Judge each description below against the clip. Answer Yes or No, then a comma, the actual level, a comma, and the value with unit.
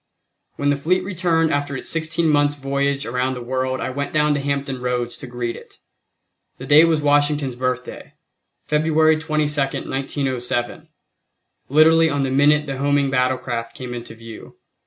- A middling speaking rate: Yes, average, 155 wpm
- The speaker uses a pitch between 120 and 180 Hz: Yes, medium, 140 Hz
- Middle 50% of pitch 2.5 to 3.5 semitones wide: Yes, average, 2.8 semitones